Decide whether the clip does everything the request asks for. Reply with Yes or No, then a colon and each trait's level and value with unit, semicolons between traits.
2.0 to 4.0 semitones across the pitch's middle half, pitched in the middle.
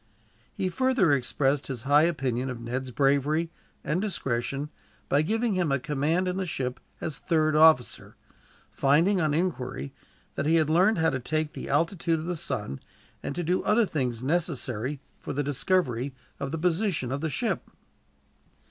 No: average, 4.5 semitones; medium, 150 Hz